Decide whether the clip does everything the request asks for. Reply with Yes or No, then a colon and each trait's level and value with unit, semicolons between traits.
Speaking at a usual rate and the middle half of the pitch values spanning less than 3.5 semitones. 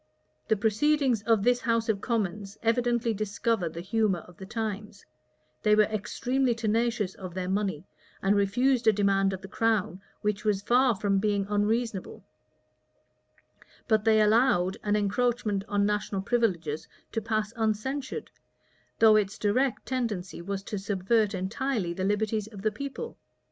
Yes: average, 150 wpm; average, 2.8 semitones